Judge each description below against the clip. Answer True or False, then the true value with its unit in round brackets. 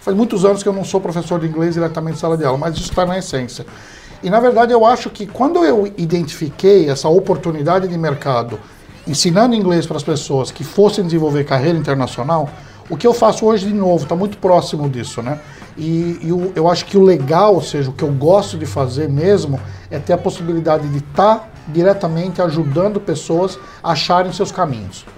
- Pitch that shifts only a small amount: False (4.5 semitones)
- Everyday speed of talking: False (205 wpm)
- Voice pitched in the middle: True (170 Hz)